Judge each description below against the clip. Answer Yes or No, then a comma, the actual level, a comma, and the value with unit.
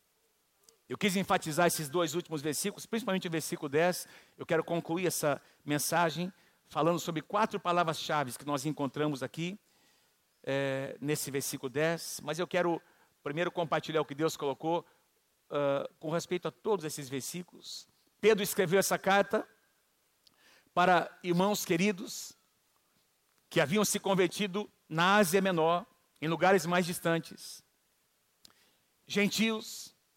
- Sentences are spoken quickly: No, average, 125 wpm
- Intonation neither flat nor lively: Yes, average, 3.9 semitones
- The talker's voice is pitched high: No, medium, 170 Hz